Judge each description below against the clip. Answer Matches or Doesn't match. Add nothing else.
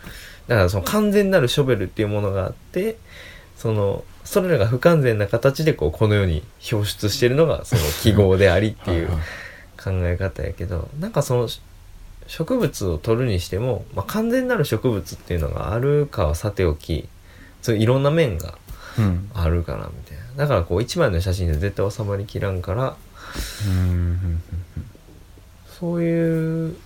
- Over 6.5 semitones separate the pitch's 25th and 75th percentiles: Doesn't match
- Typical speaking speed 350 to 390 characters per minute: Doesn't match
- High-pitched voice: Doesn't match